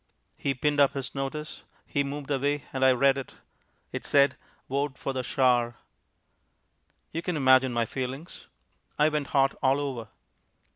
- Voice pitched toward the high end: No, low, 135 Hz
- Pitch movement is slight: Yes, narrow, 1.7 semitones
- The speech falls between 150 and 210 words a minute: Yes, average, 155 wpm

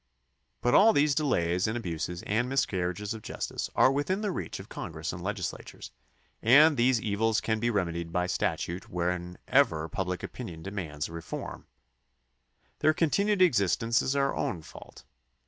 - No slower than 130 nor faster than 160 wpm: Yes, average, 150 wpm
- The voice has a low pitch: Yes, low, 105 Hz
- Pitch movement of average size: No, wide, 7.5 semitones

